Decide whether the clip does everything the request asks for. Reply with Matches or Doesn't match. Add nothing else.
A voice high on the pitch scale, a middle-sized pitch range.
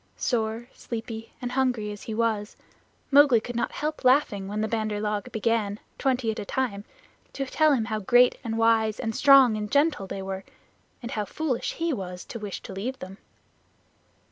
Matches